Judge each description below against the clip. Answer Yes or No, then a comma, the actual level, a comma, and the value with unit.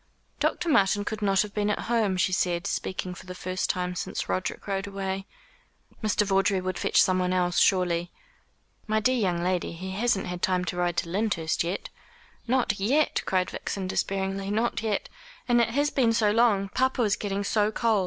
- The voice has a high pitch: Yes, high, 195 Hz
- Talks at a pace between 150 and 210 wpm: Yes, average, 190 wpm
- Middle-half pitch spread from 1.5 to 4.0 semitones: Yes, average, 2.9 semitones